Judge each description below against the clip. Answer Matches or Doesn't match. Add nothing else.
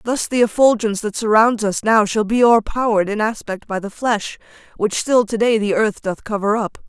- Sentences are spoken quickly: Matches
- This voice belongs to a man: Doesn't match